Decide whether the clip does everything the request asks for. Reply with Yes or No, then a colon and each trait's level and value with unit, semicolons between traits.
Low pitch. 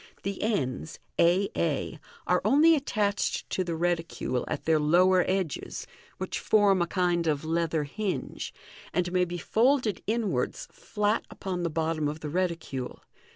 No: medium, 175 Hz